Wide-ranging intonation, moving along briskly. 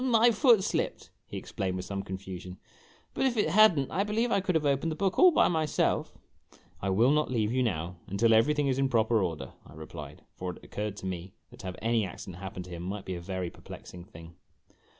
Yes: wide, 9.0 semitones; fast, 235 wpm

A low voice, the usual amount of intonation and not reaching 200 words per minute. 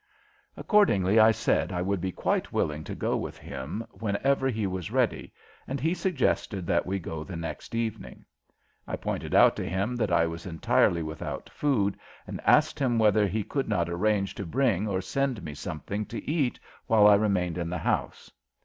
Yes: low, 100 Hz; average, 4.8 semitones; average, 185 wpm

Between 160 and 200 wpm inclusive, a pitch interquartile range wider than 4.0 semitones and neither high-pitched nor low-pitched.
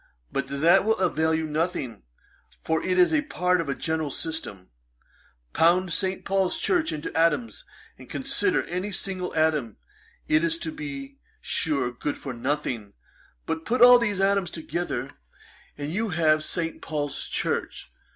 No: average, 150 wpm; average, 4.7 semitones; medium, 165 Hz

